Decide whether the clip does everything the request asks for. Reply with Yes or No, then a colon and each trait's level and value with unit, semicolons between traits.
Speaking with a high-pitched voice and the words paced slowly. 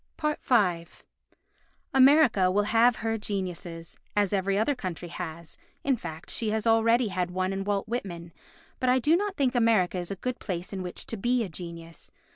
No: high, 200 Hz; average, 180 wpm